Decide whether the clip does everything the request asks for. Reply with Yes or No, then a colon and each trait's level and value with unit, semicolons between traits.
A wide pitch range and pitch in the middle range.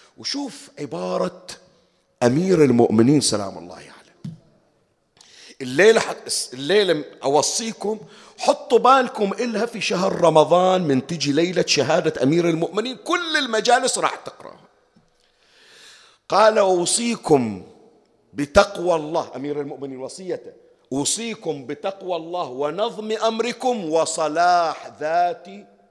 Yes: wide, 7.2 semitones; medium, 180 Hz